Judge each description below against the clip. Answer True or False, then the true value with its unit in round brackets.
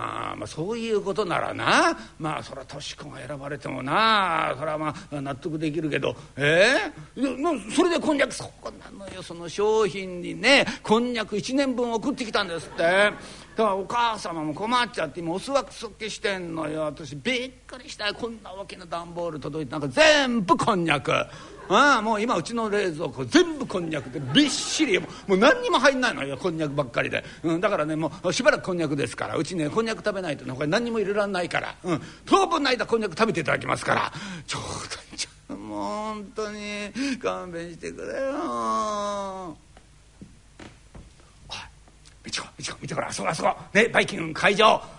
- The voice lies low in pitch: False (195 Hz)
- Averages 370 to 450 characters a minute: True (380 characters per minute)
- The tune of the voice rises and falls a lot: True (7.0 semitones)